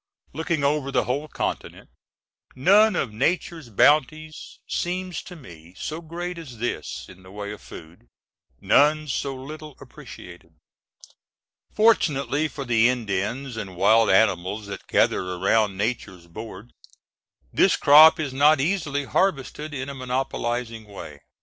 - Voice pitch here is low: Yes, low, 130 Hz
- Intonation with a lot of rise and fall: Yes, wide, 6.6 semitones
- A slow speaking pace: Yes, slow, 130 wpm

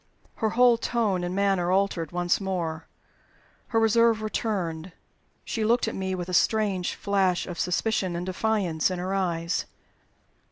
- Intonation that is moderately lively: Yes, average, 3.6 semitones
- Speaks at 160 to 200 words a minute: No, average, 150 wpm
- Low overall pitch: No, high, 190 Hz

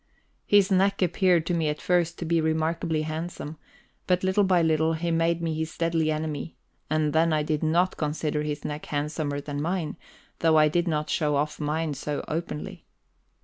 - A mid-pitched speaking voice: Yes, medium, 160 Hz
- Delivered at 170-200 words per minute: Yes, average, 185 wpm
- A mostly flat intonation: Yes, narrow, 1.9 semitones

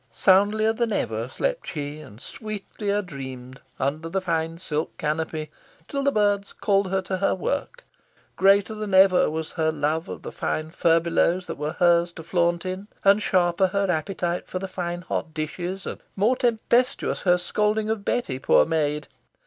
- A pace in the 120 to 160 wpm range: No, average, 170 wpm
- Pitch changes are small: No, average, 4.1 semitones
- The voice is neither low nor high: Yes, medium, 180 Hz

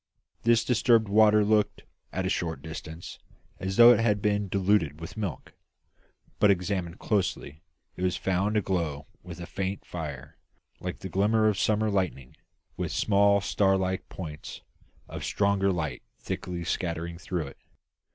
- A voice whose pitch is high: No, very low, 95 Hz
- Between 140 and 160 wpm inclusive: Yes, average, 150 wpm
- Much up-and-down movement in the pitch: No, average, 3.4 semitones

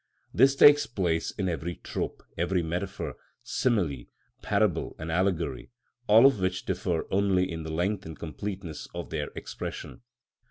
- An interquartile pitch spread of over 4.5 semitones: No, average, 3.7 semitones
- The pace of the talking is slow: No, average, 145 wpm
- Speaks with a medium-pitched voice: No, very low, 90 Hz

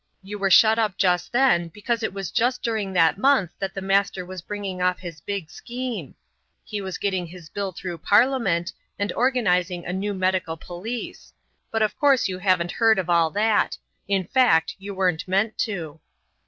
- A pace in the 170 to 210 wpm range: Yes, average, 180 wpm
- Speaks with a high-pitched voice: Yes, high, 195 Hz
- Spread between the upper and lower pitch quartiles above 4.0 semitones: No, average, 3.5 semitones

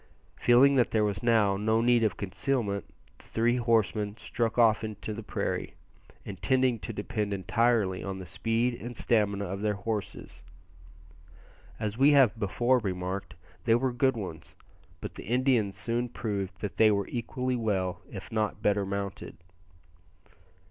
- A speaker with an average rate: Yes, average, 155 wpm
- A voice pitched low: Yes, low, 110 Hz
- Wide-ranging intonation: No, average, 3.2 semitones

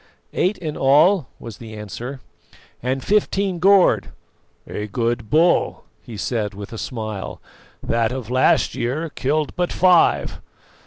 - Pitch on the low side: Yes, low, 130 Hz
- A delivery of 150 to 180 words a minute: No, slow, 135 wpm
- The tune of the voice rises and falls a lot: Yes, wide, 6.8 semitones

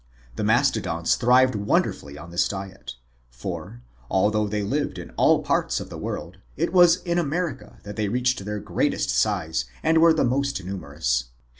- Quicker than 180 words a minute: No, average, 165 wpm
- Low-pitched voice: Yes, low, 105 Hz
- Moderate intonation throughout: No, wide, 7.3 semitones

